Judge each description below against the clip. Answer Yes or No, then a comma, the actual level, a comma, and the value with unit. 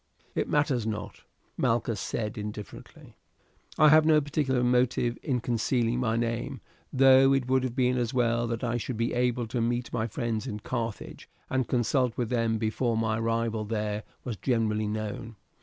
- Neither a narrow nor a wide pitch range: No, narrow, 2.1 semitones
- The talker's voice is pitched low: Yes, low, 120 Hz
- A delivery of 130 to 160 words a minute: No, average, 170 wpm